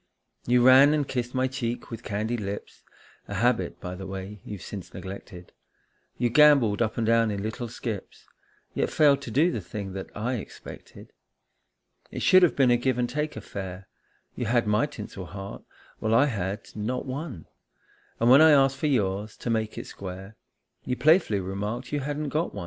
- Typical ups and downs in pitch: Yes, average, 4.7 semitones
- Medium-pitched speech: No, low, 115 Hz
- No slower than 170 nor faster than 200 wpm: Yes, average, 185 wpm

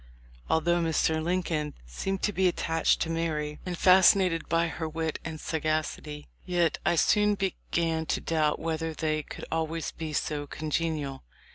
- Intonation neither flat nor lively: No, narrow, 1.8 semitones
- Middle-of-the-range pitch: Yes, medium, 160 Hz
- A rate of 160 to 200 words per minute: No, average, 150 wpm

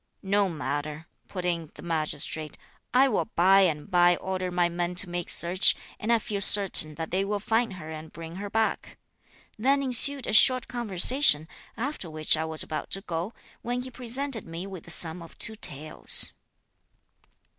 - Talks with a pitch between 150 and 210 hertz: Yes, medium, 185 Hz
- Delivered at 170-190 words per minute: Yes, average, 175 wpm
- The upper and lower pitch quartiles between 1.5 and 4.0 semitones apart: No, average, 5.3 semitones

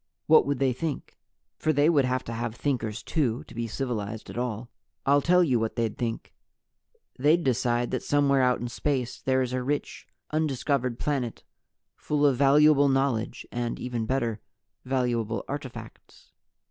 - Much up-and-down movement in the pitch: No, average, 3.2 semitones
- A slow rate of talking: No, average, 160 wpm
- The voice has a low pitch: Yes, low, 130 Hz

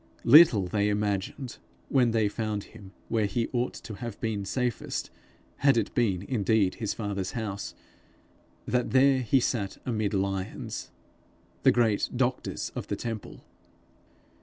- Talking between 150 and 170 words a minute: No, slow, 135 wpm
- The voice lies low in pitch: Yes, low, 110 Hz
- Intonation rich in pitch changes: No, average, 3.3 semitones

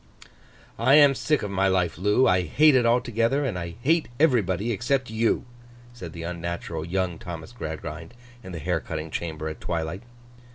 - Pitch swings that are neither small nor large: No, wide, 6.2 semitones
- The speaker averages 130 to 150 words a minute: No, average, 170 wpm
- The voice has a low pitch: Yes, very low, 95 Hz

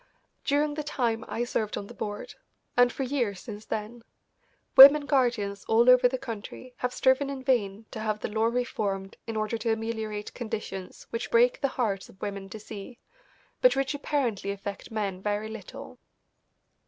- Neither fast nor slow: Yes, average, 170 wpm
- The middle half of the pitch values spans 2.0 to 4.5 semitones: Yes, average, 3.4 semitones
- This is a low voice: No, high, 225 Hz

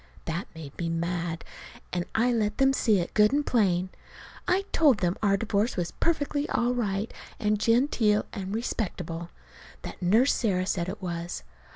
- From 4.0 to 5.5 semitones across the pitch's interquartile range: Yes, average, 5.1 semitones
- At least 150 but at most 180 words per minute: Yes, average, 165 wpm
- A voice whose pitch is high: Yes, high, 205 Hz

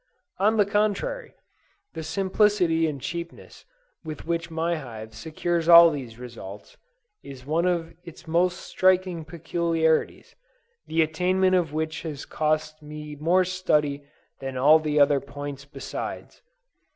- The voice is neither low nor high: Yes, medium, 160 Hz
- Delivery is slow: Yes, slow, 130 wpm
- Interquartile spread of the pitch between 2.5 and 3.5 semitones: Yes, average, 3.0 semitones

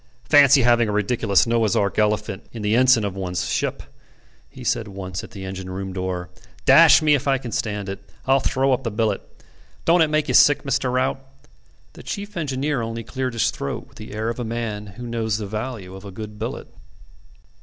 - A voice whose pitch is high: No, low, 115 Hz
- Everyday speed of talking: No, fast, 210 wpm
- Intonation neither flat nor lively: Yes, average, 4.4 semitones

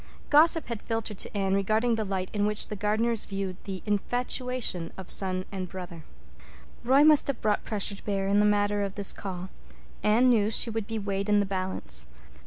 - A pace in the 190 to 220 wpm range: Yes, average, 195 wpm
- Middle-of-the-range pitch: No, high, 205 Hz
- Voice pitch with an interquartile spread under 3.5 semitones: Yes, average, 2.7 semitones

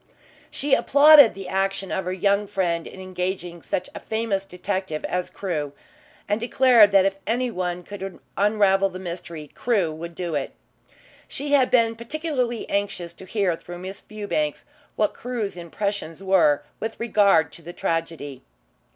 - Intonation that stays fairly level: No, average, 3.7 semitones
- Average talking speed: Yes, average, 150 wpm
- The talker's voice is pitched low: No, high, 195 Hz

